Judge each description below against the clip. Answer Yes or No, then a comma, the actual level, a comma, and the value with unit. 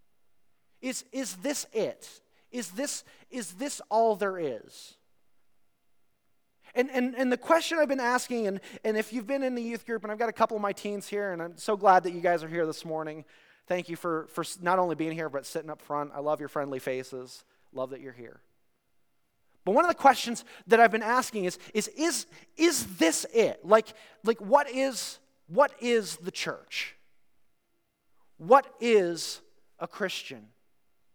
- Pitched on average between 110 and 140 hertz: No, high, 215 Hz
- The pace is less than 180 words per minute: No, average, 185 wpm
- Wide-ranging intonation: Yes, wide, 7.1 semitones